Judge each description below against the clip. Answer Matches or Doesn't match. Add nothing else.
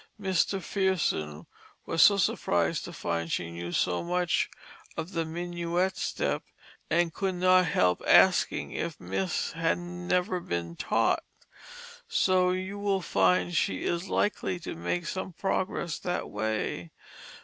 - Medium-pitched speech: Matches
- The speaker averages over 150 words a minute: Doesn't match